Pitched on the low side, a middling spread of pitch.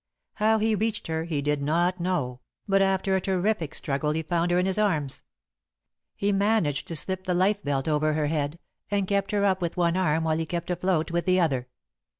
No: medium, 175 Hz; average, 3.9 semitones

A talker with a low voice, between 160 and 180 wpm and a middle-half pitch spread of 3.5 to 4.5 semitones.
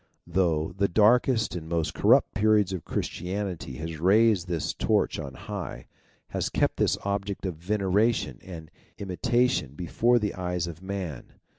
No: very low, 95 Hz; average, 140 wpm; average, 3.9 semitones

